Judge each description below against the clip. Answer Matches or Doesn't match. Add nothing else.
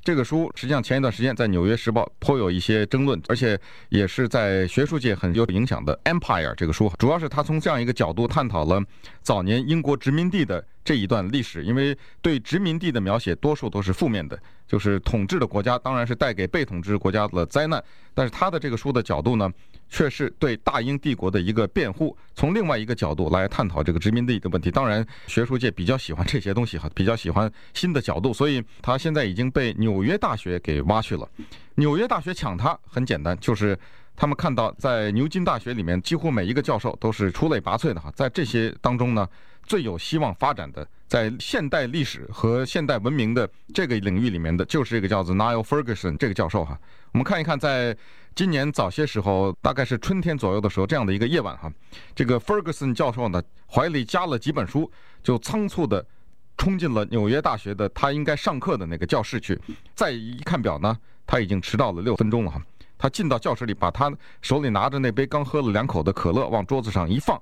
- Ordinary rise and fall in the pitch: Doesn't match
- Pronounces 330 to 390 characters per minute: Matches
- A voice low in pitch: Matches